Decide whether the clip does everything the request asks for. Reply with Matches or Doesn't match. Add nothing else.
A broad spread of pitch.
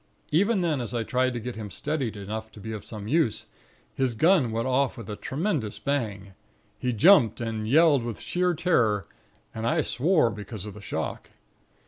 Matches